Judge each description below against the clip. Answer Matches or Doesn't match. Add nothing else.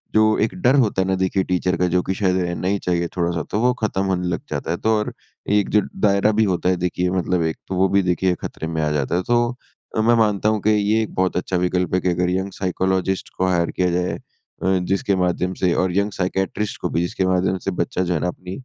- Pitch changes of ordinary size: Doesn't match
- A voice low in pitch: Matches